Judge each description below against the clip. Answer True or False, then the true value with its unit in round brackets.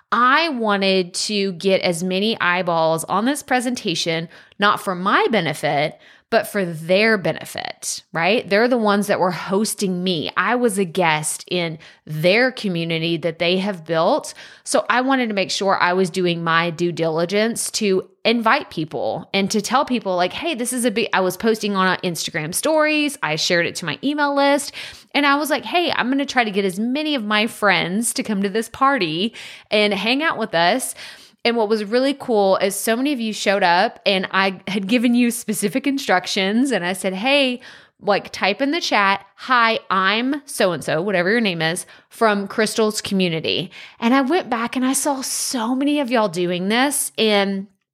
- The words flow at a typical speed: True (195 wpm)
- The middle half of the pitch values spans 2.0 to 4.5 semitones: False (5.2 semitones)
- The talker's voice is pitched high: True (210 Hz)